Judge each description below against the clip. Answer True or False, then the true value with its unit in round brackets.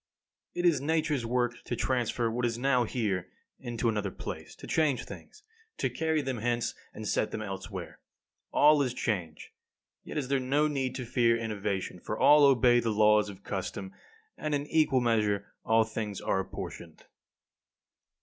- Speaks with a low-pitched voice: True (120 Hz)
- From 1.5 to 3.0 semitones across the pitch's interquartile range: False (4.2 semitones)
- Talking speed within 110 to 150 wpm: False (170 wpm)